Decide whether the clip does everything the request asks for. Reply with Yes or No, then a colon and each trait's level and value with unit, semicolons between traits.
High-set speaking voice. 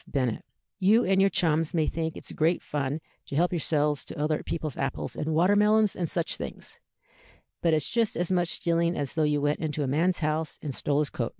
No: medium, 160 Hz